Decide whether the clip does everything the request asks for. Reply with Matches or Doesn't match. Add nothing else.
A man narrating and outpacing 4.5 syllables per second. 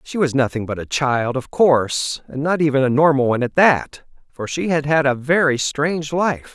Matches